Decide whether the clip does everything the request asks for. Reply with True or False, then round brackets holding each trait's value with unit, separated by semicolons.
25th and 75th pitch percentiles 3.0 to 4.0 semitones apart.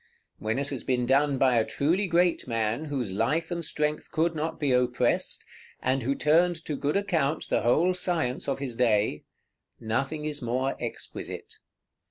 False (4.4 semitones)